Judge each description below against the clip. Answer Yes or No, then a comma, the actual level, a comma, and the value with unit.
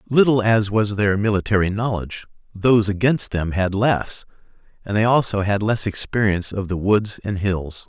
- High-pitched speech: No, low, 105 Hz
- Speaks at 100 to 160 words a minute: No, average, 170 wpm